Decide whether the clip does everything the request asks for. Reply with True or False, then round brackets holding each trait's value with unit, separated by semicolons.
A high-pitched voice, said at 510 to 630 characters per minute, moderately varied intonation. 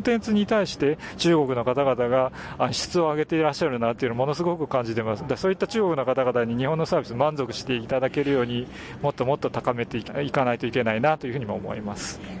False (130 Hz; 515 characters per minute; 4.4 semitones)